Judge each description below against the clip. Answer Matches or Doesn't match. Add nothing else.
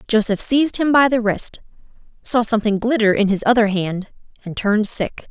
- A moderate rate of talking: Matches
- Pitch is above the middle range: Matches